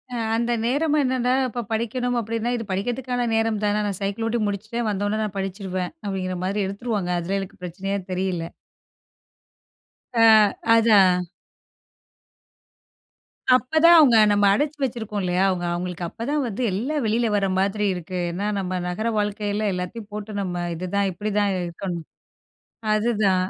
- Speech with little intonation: No, average, 3.6 semitones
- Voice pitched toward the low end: No, high, 205 Hz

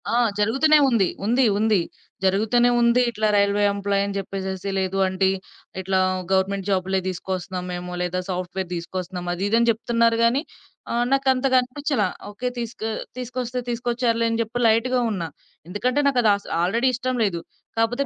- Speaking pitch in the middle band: No, high, 215 Hz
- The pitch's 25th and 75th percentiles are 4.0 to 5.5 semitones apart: Yes, average, 4.3 semitones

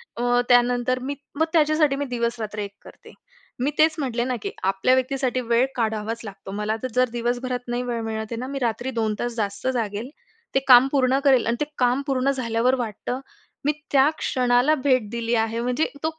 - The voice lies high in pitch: Yes, high, 245 Hz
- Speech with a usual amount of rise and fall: No, narrow, 2.3 semitones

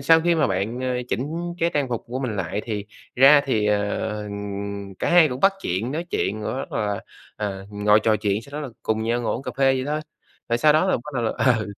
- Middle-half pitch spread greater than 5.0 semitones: Yes, wide, 5.6 semitones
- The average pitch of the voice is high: No, low, 120 Hz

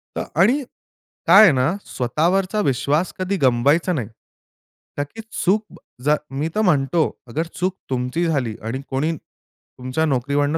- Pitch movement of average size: No, wide, 5.7 semitones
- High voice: No, medium, 150 Hz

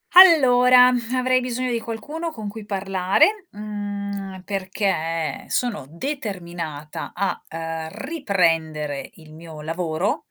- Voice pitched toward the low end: No, high, 200 Hz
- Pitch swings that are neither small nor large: No, wide, 7.1 semitones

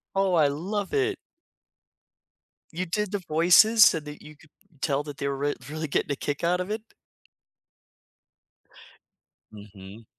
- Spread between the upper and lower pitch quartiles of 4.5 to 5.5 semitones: Yes, average, 5.1 semitones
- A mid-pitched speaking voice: Yes, medium, 160 Hz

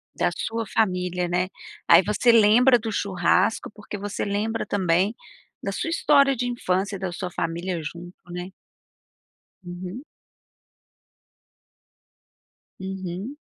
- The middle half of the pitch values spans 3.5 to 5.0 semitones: Yes, average, 3.8 semitones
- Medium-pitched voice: No, high, 195 Hz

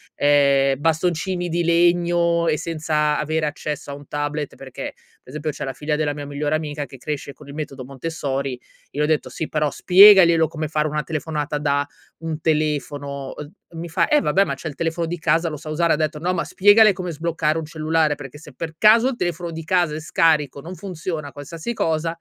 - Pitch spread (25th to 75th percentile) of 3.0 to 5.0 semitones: No, narrow, 2.4 semitones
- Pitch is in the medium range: Yes, medium, 155 Hz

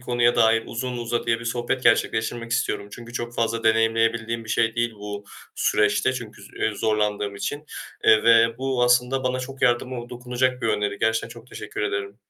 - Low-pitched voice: Yes, low, 115 Hz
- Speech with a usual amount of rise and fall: No, narrow, 1.7 semitones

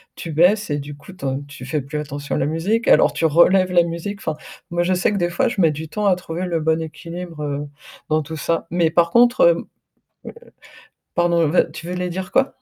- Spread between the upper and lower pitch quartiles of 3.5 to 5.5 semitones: No, average, 3.0 semitones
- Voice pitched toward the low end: No, medium, 170 Hz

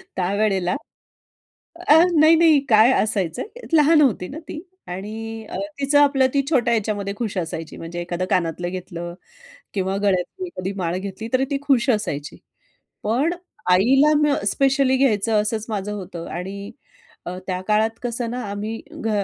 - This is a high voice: Yes, high, 215 Hz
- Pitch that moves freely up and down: Yes, wide, 6.1 semitones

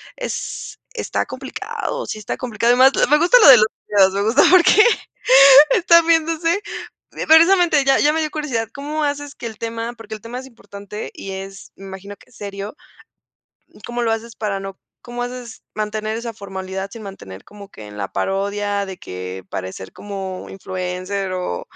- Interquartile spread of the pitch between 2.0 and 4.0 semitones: No, wide, 5.6 semitones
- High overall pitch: Yes, high, 215 Hz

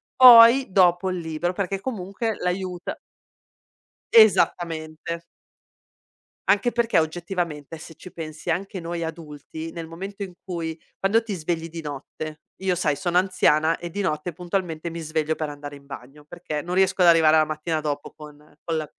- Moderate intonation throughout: Yes, average, 3.1 semitones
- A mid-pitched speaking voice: Yes, medium, 170 Hz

